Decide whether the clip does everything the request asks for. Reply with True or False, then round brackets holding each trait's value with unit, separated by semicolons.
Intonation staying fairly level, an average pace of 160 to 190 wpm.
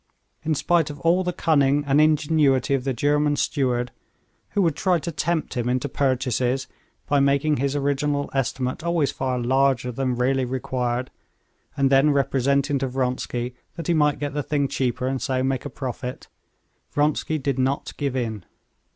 True (2.3 semitones; 170 wpm)